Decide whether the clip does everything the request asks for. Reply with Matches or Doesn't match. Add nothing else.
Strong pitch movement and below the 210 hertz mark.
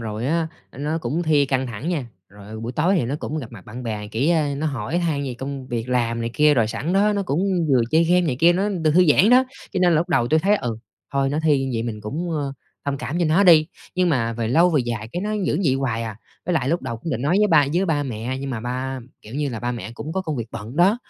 Matches